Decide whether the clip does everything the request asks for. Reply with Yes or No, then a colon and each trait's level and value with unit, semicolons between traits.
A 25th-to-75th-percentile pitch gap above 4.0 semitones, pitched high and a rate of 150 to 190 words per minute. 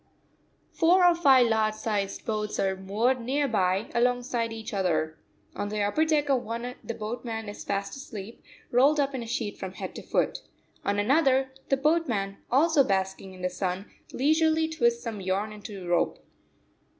Yes: average, 5.2 semitones; high, 230 Hz; average, 170 wpm